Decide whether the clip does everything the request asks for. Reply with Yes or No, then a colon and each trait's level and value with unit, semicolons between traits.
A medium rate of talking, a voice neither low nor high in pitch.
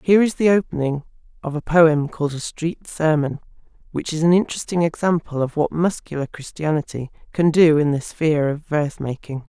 Yes: average, 175 wpm; medium, 155 Hz